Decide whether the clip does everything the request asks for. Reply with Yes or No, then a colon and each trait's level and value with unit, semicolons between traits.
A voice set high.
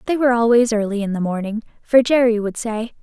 Yes: high, 225 Hz